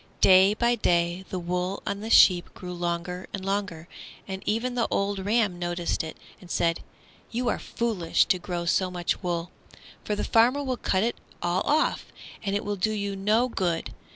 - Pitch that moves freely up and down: No, average, 3.5 semitones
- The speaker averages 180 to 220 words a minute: Yes, average, 185 wpm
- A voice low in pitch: No, high, 190 Hz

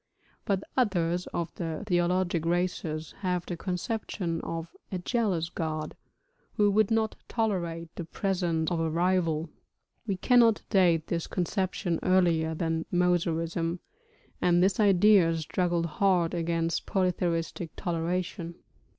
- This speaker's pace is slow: Yes, slow, 120 wpm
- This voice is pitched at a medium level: Yes, medium, 175 Hz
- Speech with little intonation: Yes, narrow, 2.1 semitones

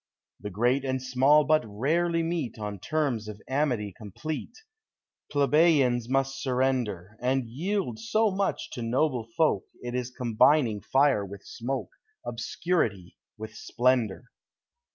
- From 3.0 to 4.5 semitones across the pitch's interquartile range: No, average, 5.2 semitones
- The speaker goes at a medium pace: No, slow, 125 wpm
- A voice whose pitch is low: Yes, low, 130 Hz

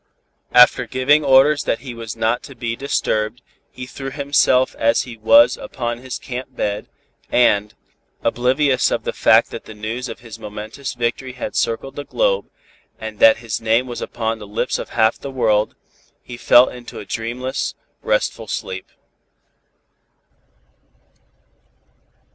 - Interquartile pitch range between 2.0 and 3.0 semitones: Yes, average, 2.7 semitones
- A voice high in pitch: No, low, 120 Hz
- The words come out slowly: No, average, 150 wpm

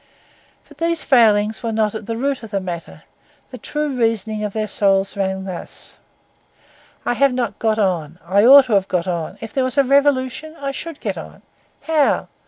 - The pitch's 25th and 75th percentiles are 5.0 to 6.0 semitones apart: Yes, wide, 5.5 semitones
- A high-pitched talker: Yes, high, 225 Hz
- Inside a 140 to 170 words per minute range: No, average, 190 wpm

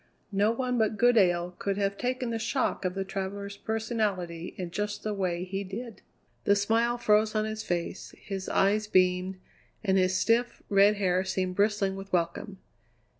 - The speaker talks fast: No, average, 170 wpm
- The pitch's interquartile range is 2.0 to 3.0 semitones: Yes, narrow, 2.6 semitones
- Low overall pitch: No, high, 200 Hz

